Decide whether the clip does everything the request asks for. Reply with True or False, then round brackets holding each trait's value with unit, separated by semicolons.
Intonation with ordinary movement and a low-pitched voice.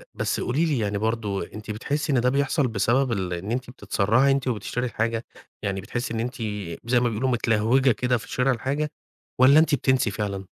True (3.6 semitones; 120 Hz)